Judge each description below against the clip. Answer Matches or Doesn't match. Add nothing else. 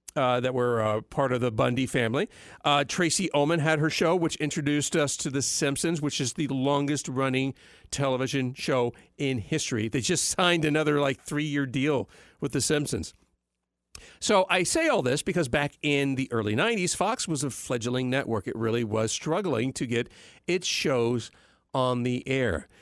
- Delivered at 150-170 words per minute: Doesn't match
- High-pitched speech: Doesn't match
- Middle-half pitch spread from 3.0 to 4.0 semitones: Matches